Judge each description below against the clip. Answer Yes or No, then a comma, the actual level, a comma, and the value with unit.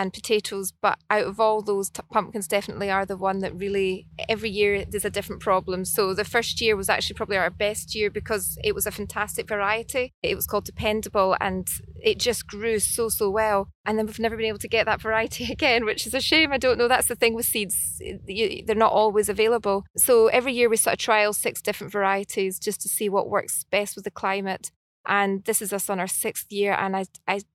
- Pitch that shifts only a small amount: Yes, narrow, 2.1 semitones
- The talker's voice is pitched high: Yes, high, 210 Hz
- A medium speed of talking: No, fast, 230 wpm